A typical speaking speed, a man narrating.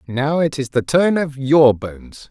No: fast, 210 wpm; male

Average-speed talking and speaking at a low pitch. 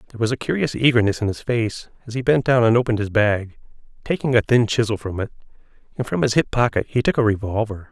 No: fast, 235 wpm; low, 115 Hz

